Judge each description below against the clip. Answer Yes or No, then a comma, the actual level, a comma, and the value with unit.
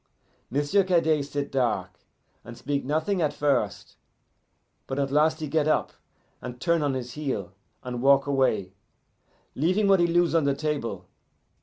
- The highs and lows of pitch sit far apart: No, average, 3.7 semitones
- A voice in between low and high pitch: Yes, medium, 145 Hz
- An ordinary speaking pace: Yes, average, 155 wpm